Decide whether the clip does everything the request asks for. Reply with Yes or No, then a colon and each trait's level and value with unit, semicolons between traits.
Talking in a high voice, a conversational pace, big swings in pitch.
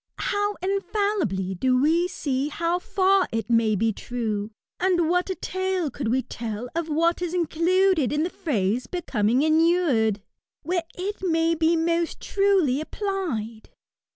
Yes: very high, 325 Hz; average, 150 wpm; wide, 7.0 semitones